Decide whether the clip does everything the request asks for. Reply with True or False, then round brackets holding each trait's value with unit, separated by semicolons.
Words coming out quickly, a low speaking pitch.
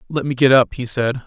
True (285 wpm; 130 Hz)